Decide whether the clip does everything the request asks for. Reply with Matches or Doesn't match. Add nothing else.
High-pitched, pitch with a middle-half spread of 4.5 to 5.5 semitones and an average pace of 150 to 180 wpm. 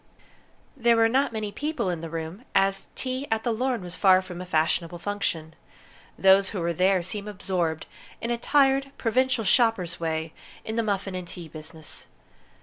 Matches